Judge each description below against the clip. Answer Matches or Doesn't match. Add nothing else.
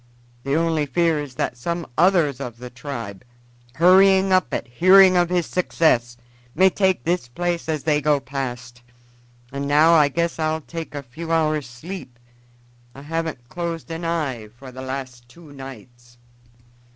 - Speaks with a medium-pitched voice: Matches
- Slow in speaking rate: Doesn't match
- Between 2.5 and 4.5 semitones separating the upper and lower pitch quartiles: Doesn't match